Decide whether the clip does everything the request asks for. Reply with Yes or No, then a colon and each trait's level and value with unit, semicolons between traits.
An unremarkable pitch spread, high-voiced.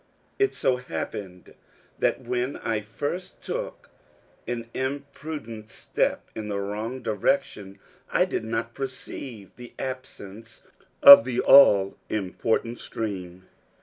No: average, 4.0 semitones; low, 115 Hz